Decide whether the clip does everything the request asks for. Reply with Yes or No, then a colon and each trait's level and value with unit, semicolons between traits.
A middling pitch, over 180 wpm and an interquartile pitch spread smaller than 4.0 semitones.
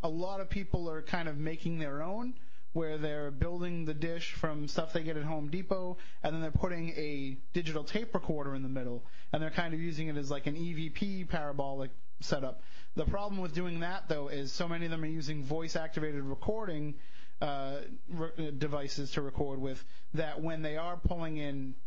Yes: medium, 160 Hz; average, 200 wpm; average, 2.9 semitones